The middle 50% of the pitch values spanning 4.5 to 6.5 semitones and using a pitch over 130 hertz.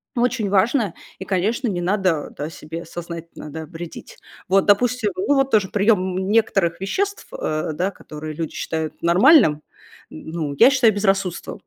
Yes: average, 4.8 semitones; high, 190 Hz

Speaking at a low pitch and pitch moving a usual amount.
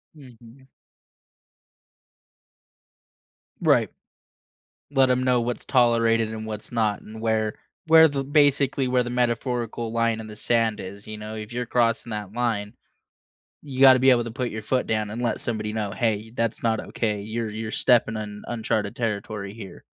No: low, 115 Hz; narrow, 2.3 semitones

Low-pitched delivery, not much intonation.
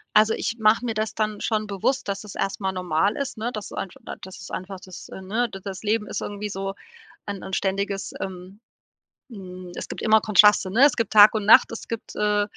No: high, 205 Hz; narrow, 2.2 semitones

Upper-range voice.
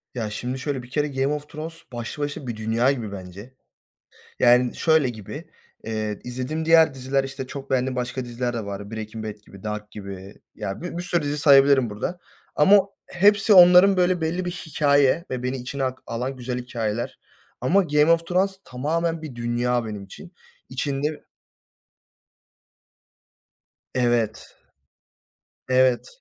No: low, 130 Hz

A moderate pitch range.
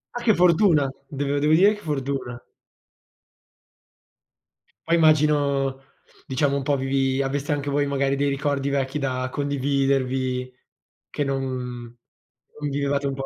No: narrow, 1.4 semitones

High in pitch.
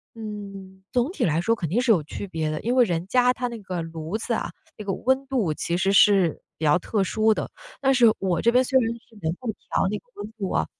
Yes: high, 210 Hz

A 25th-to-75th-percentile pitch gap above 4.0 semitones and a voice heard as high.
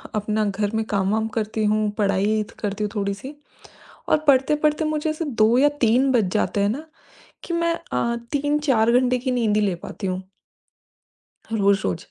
Yes: average, 4.8 semitones; high, 220 Hz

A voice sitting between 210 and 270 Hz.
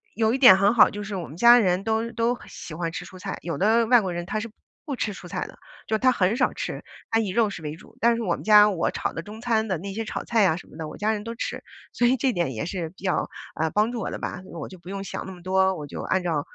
No: high, 200 Hz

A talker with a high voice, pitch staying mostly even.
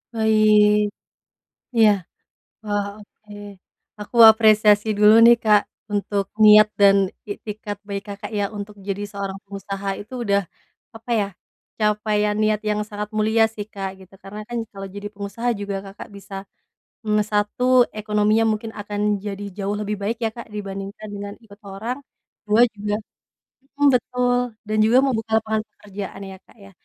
Yes: high, 210 Hz; narrow, 1.3 semitones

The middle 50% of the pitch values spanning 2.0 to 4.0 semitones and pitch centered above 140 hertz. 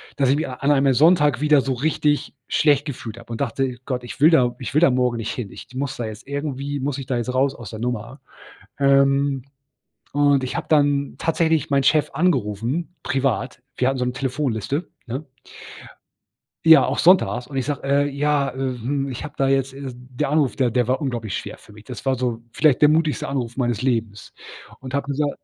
No: narrow, 2.5 semitones; low, 135 Hz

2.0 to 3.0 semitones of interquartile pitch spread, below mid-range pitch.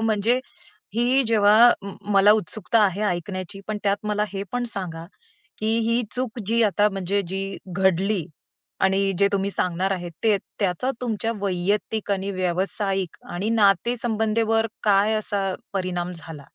No: narrow, 2.5 semitones; high, 200 Hz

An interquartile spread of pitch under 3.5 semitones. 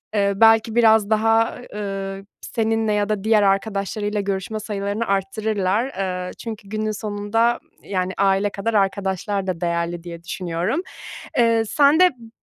Yes: narrow, 2.4 semitones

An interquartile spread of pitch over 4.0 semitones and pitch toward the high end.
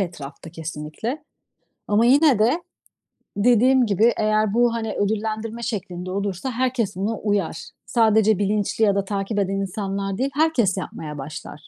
No: average, 3.2 semitones; high, 210 Hz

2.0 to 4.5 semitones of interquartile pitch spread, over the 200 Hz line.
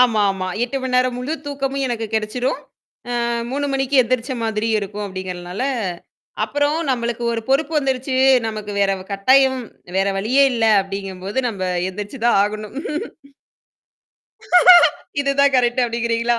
Yes: average, 4.2 semitones; high, 235 Hz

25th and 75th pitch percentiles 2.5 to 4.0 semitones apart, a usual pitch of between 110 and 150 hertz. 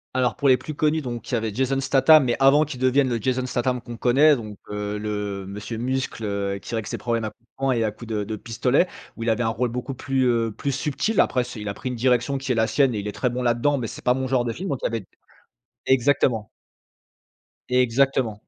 Yes: average, 2.9 semitones; low, 125 Hz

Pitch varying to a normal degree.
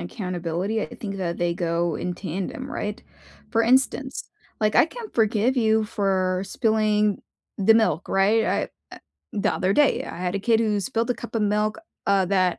Yes: average, 3.4 semitones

